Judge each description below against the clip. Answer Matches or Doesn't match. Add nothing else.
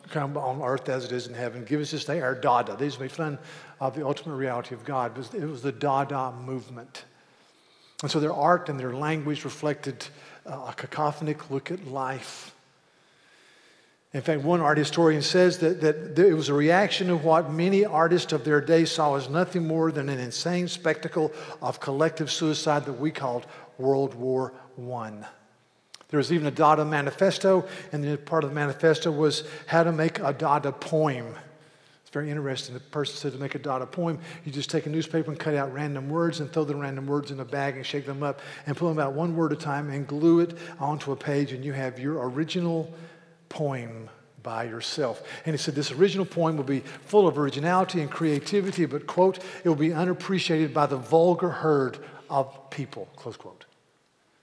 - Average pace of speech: Matches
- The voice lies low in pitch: Doesn't match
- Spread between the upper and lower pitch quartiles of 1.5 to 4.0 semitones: Matches